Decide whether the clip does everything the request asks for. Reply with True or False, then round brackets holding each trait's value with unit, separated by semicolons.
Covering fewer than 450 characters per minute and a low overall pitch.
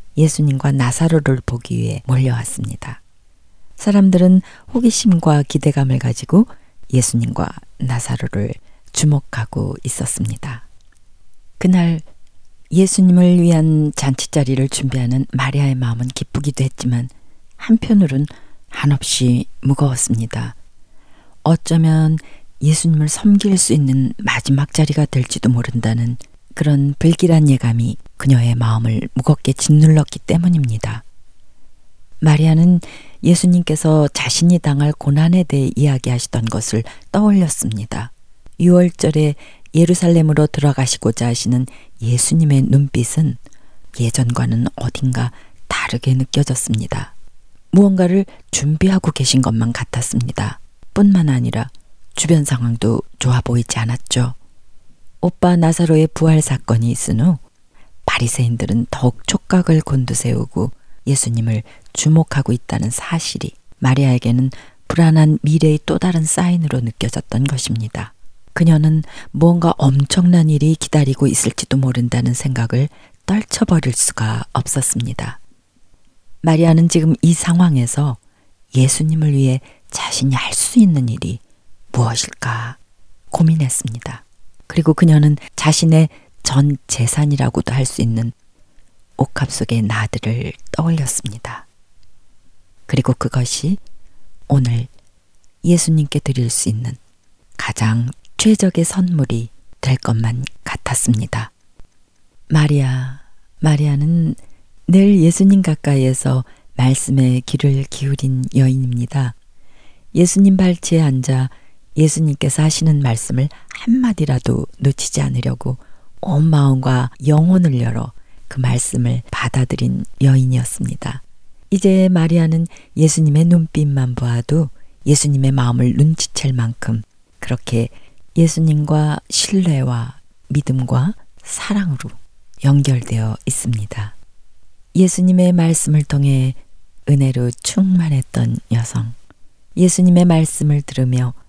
True (265 characters per minute; 130 Hz)